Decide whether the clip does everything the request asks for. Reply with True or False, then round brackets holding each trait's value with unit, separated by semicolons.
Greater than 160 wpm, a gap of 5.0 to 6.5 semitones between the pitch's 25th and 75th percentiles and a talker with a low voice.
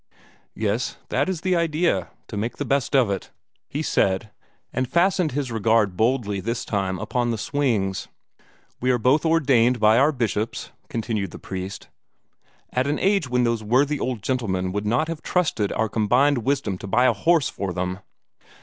True (175 wpm; 5.5 semitones; 120 Hz)